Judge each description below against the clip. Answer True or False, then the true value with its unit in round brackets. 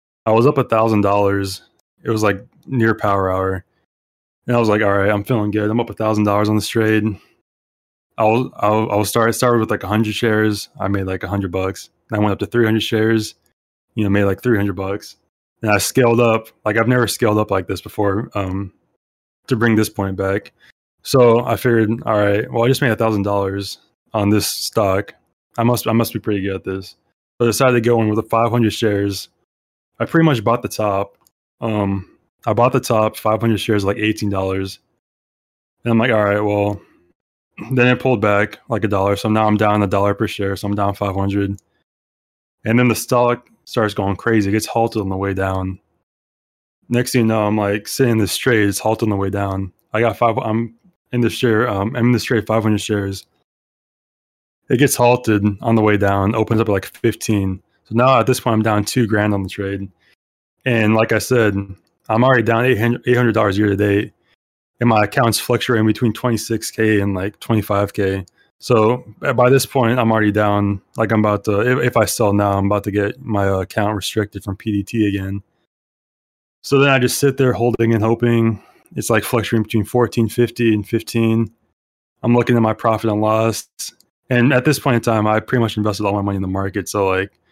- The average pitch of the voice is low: True (110 Hz)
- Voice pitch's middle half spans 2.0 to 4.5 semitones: True (2.6 semitones)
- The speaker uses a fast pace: True (215 wpm)